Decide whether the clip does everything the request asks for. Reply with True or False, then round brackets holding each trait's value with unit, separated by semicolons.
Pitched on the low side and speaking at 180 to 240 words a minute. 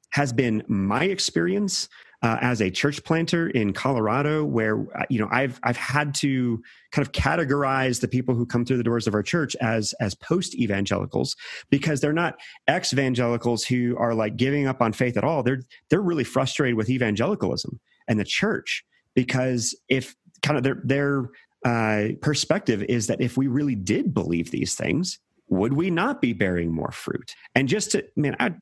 True (130 Hz; 185 wpm)